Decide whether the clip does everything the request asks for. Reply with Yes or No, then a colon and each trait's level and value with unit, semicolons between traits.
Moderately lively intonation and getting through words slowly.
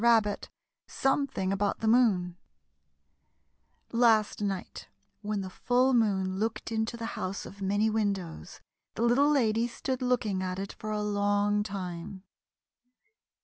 Yes: average, 3.1 semitones; slow, 130 wpm